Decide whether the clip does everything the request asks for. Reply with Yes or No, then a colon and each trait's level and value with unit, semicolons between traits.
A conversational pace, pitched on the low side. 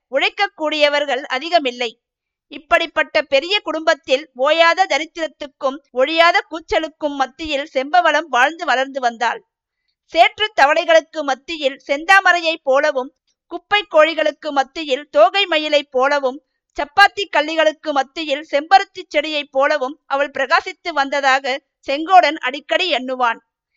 No: average, 95 wpm; very high, 300 Hz